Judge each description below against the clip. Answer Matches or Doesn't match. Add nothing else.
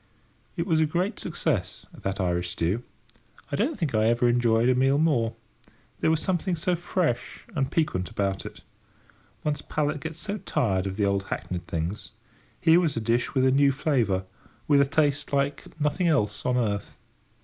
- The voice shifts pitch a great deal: Matches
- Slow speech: Doesn't match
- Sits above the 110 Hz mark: Matches